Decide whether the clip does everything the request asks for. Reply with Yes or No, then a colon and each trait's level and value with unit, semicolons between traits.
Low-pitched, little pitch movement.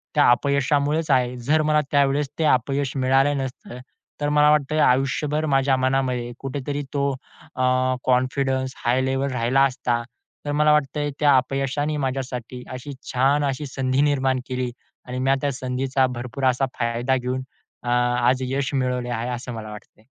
Yes: low, 130 Hz; narrow, 2.0 semitones